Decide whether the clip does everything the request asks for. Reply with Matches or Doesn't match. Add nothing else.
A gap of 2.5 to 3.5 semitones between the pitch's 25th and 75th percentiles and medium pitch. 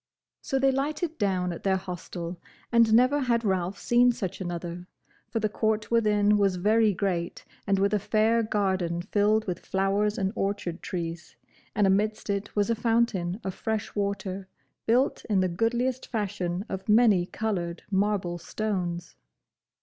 Doesn't match